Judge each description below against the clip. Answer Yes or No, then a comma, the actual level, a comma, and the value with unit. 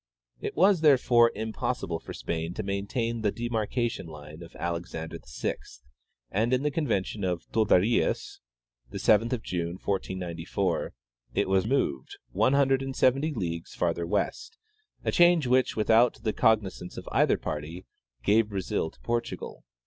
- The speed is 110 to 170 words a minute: Yes, average, 145 wpm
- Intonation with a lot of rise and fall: Yes, wide, 5.8 semitones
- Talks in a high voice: No, low, 110 Hz